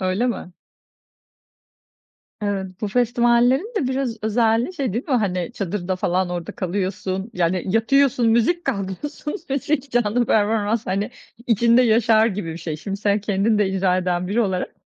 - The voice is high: Yes, high, 210 Hz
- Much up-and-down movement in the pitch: No, average, 4.2 semitones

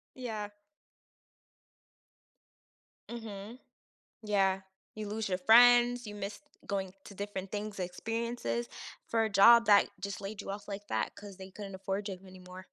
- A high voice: Yes, high, 205 Hz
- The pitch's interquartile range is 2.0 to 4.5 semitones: Yes, narrow, 2.5 semitones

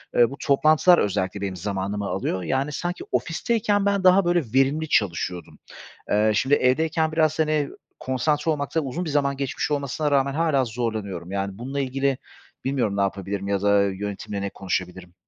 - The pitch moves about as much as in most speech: No, wide, 7.4 semitones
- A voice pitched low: Yes, low, 130 Hz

